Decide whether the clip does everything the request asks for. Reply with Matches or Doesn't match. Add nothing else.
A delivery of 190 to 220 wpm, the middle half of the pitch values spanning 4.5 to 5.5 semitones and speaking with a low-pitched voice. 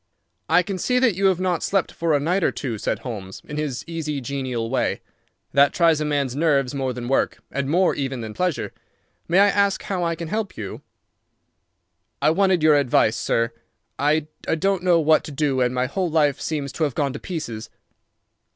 Doesn't match